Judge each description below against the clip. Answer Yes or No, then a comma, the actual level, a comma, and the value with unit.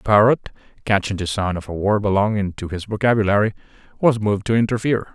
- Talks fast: No, average, 185 wpm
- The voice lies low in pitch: Yes, low, 105 Hz